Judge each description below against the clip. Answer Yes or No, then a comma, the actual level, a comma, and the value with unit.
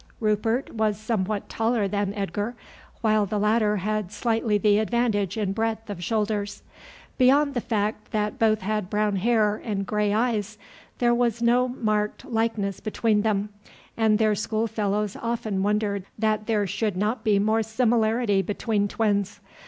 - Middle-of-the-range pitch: No, high, 215 Hz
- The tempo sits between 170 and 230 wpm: No, average, 150 wpm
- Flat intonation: Yes, narrow, 1.6 semitones